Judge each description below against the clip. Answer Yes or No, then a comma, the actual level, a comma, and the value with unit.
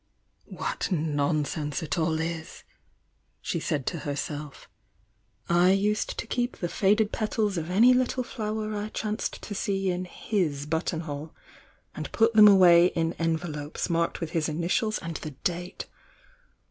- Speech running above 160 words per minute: No, average, 145 wpm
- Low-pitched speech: No, medium, 175 Hz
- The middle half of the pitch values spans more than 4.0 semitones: Yes, average, 4.9 semitones